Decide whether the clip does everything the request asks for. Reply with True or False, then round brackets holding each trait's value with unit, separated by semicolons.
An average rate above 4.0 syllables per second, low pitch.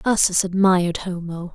False (5.0 syllables/s; 180 Hz)